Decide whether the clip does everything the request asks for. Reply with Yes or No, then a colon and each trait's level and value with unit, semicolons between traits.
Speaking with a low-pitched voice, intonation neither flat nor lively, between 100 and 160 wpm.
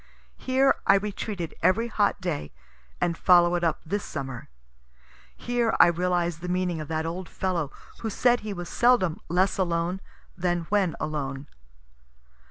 No: medium, 180 Hz; average, 3.3 semitones; average, 150 wpm